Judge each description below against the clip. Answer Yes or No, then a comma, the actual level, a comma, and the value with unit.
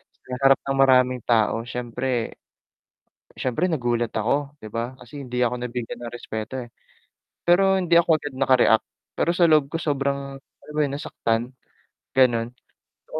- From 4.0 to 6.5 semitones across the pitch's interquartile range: No, average, 3.2 semitones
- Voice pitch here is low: Yes, low, 130 Hz